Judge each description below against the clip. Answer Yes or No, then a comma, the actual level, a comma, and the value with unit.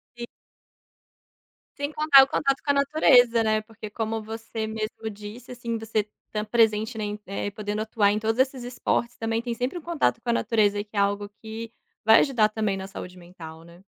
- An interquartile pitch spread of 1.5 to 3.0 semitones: Yes, narrow, 2.5 semitones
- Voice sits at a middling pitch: No, high, 220 Hz